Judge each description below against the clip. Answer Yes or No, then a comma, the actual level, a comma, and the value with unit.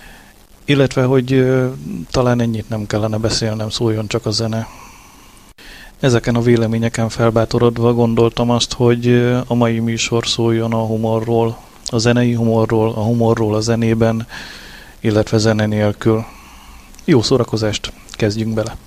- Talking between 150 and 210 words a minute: No, average, 125 wpm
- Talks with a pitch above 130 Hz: No, low, 115 Hz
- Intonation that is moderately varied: No, narrow, 1.3 semitones